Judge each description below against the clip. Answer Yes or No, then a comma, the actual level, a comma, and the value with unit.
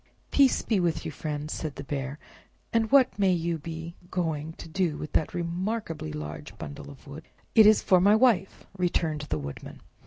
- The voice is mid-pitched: Yes, medium, 165 Hz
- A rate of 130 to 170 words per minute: No, average, 185 wpm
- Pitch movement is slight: No, average, 4.2 semitones